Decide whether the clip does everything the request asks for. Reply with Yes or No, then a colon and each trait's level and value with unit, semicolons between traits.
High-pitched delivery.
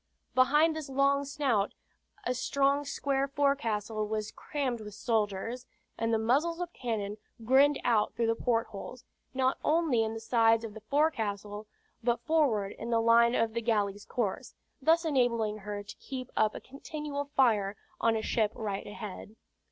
Yes: high, 235 Hz